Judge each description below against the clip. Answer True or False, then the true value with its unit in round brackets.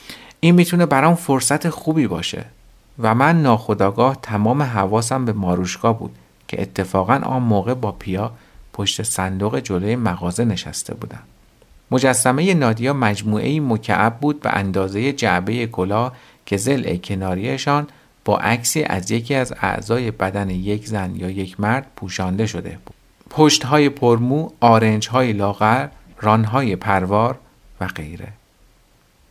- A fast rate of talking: False (130 wpm)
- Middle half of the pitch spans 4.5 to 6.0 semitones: True (5.1 semitones)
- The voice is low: True (110 Hz)